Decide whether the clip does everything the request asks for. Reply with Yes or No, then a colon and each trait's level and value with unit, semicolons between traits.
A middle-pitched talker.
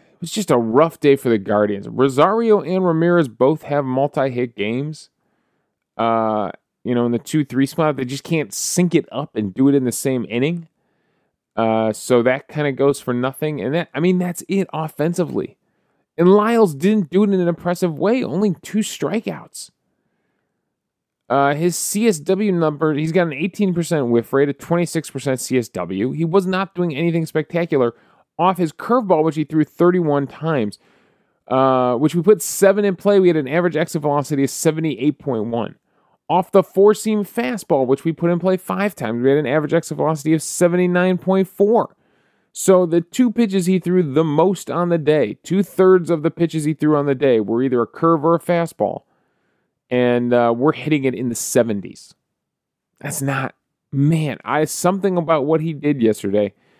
Yes: medium, 155 Hz